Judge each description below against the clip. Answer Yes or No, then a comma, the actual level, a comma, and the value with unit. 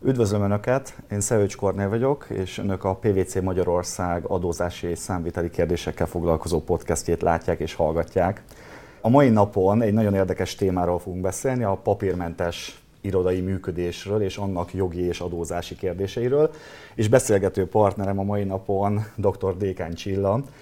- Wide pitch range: No, narrow, 2.5 semitones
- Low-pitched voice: Yes, very low, 95 Hz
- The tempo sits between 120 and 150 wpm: Yes, average, 140 wpm